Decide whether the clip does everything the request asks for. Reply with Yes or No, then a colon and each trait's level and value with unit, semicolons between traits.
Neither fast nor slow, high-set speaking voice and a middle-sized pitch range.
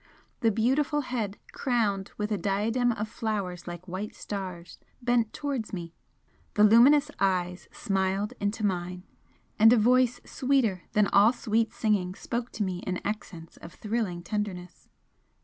Yes: average, 145 wpm; high, 210 Hz; average, 4.0 semitones